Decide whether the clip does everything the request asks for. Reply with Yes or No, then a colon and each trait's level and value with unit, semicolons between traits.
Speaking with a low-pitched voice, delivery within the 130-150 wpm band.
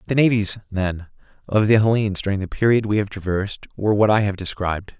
No: low, 100 Hz; fast, 205 wpm